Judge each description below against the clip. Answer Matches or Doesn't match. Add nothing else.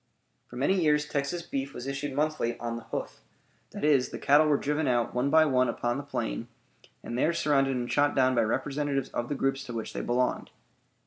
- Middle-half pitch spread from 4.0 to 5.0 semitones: Doesn't match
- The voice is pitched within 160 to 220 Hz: Doesn't match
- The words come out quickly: Matches